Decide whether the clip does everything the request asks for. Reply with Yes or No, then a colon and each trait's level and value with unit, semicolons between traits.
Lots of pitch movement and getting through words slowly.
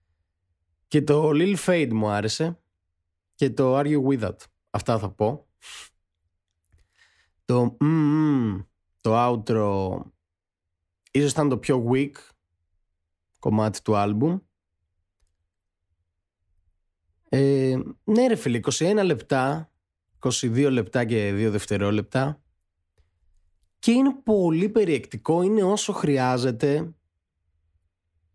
Yes: wide, 8.5 semitones; slow, 95 wpm